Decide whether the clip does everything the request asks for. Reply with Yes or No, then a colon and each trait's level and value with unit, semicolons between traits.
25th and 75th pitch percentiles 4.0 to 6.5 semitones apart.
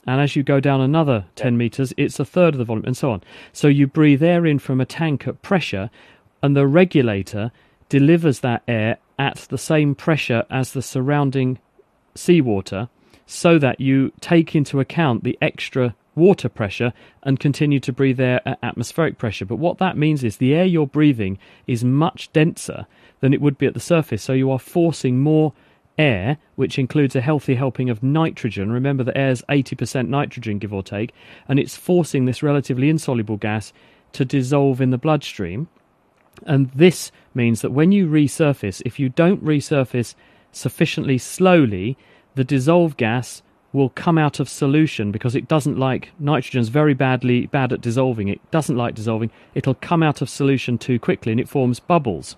No: average, 3.6 semitones